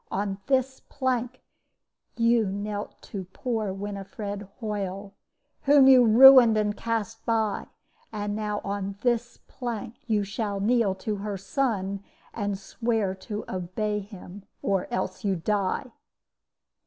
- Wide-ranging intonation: No, average, 2.9 semitones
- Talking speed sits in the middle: No, slow, 125 wpm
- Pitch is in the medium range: No, high, 210 Hz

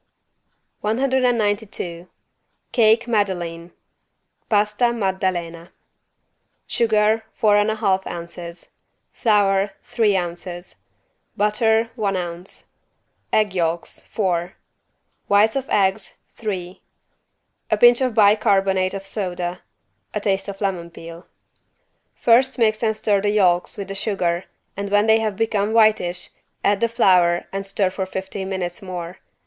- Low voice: No, high, 200 Hz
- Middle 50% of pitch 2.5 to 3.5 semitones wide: Yes, average, 3.2 semitones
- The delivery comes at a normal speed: No, slow, 120 wpm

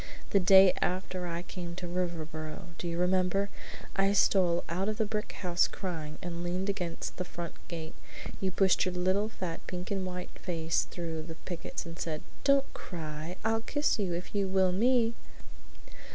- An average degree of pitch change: No, narrow, 2.3 semitones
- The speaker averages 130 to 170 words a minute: No, average, 180 wpm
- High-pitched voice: No, medium, 180 Hz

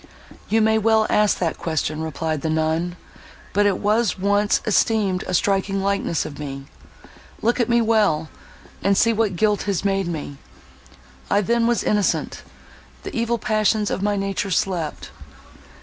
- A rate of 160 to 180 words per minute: No, average, 150 wpm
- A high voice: Yes, high, 200 Hz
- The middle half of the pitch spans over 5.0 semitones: No, average, 4.1 semitones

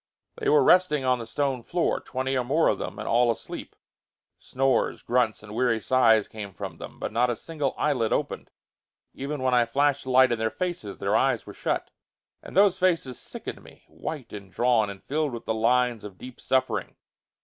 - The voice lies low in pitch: Yes, low, 125 Hz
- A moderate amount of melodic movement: Yes, average, 4.0 semitones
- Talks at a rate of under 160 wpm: No, average, 200 wpm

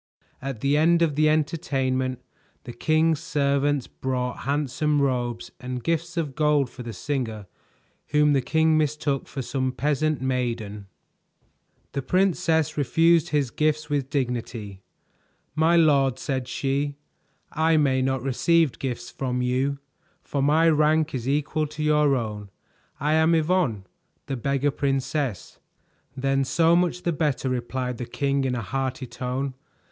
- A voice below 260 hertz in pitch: Yes, medium, 140 Hz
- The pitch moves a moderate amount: Yes, average, 3.2 semitones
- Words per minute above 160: No, average, 140 wpm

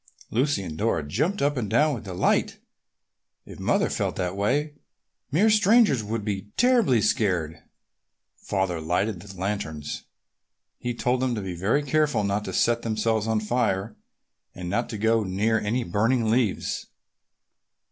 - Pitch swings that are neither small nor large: Yes, average, 4.7 semitones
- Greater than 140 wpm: Yes, average, 150 wpm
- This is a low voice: Yes, low, 110 Hz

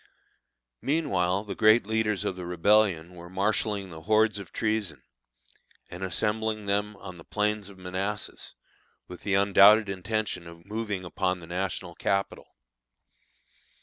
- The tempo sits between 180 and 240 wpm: No, slow, 135 wpm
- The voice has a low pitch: Yes, low, 100 Hz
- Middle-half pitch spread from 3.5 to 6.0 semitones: No, average, 2.8 semitones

